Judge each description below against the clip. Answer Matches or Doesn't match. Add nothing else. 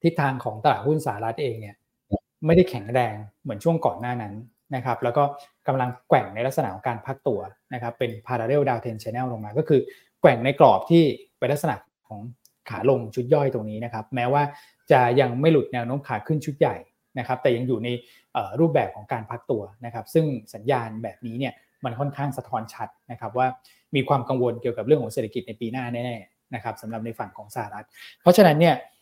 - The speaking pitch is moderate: Doesn't match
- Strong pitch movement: Doesn't match